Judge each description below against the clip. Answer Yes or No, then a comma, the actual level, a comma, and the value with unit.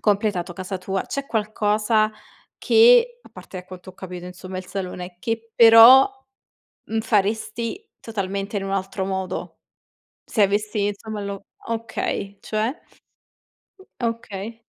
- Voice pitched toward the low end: No, high, 205 Hz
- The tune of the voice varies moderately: Yes, average, 3.0 semitones